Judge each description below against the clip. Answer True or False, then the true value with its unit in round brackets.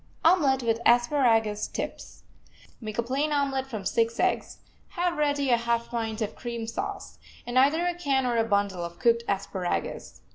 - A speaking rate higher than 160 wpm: True (170 wpm)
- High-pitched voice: True (240 Hz)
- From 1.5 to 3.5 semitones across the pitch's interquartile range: False (3.9 semitones)